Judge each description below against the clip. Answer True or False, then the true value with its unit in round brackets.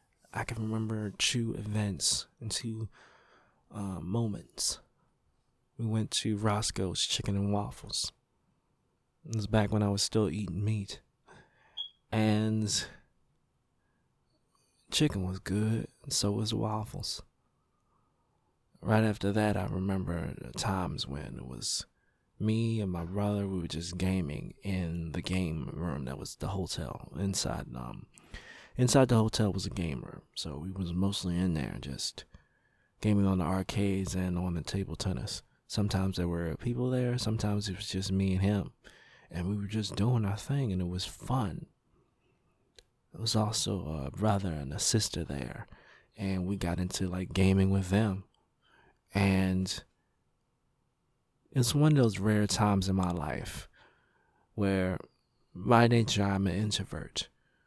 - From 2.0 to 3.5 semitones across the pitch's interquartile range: True (2.8 semitones)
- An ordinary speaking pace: True (145 wpm)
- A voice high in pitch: False (100 Hz)